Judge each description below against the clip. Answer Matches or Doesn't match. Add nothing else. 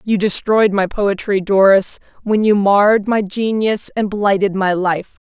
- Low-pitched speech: Doesn't match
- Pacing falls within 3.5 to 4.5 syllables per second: Matches